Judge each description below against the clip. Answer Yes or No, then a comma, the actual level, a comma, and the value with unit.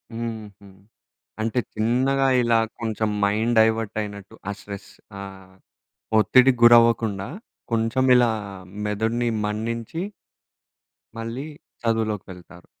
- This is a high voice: No, low, 110 Hz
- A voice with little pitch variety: Yes, narrow, 2.2 semitones